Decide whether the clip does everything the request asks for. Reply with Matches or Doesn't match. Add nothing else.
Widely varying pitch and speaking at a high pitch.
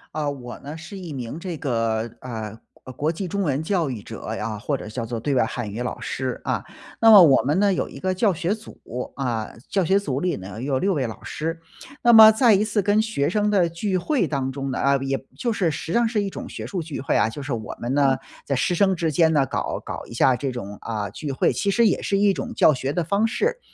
Doesn't match